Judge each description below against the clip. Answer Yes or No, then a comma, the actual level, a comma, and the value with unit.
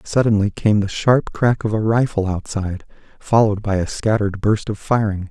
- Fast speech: No, average, 180 wpm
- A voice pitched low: Yes, low, 105 Hz